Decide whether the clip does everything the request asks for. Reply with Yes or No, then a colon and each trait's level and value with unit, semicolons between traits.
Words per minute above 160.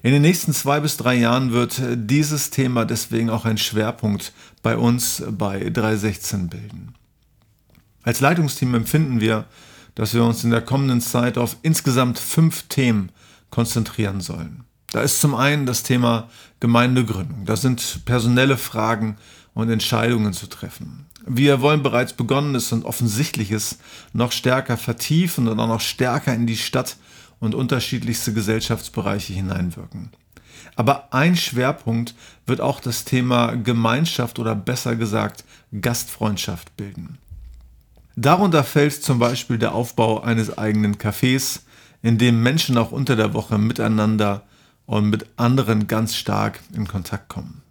No: average, 135 wpm